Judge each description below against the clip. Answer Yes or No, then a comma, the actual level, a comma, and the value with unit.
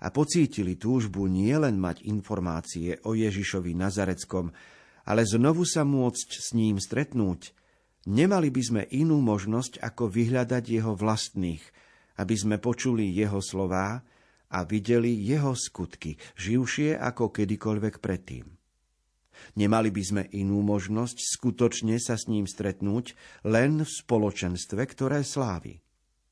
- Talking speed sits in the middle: Yes, average, 120 wpm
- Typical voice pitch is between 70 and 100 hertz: No, low, 110 Hz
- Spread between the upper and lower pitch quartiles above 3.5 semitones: Yes, average, 4.1 semitones